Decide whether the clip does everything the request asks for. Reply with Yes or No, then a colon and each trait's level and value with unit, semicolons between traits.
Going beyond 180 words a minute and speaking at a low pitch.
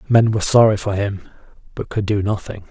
Yes: average, 200 wpm; low, 105 Hz